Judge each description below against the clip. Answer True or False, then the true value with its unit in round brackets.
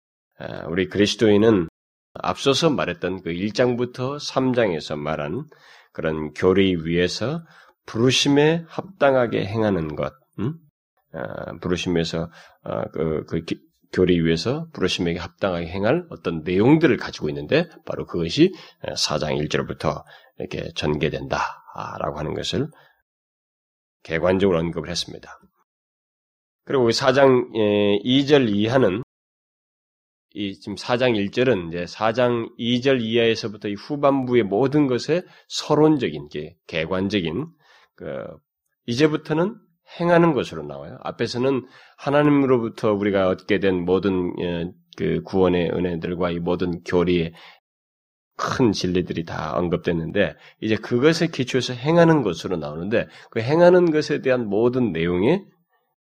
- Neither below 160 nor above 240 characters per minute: False (265 characters per minute)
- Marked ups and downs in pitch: True (7.2 semitones)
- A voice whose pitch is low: True (105 Hz)